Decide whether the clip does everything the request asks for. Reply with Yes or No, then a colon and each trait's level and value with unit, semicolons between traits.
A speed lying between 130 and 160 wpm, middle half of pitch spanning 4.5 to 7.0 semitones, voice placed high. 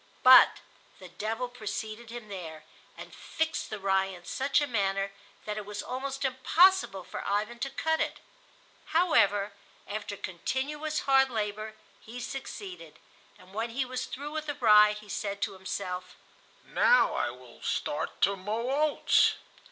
Yes: average, 150 wpm; average, 5.1 semitones; high, 220 Hz